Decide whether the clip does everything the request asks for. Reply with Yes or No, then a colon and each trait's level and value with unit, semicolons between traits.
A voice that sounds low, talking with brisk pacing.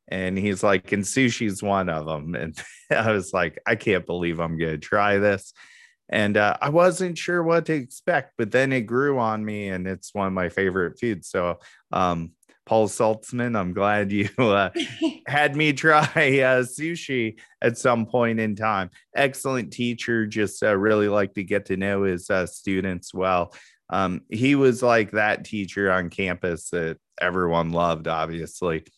No: low, 105 Hz; average, 175 wpm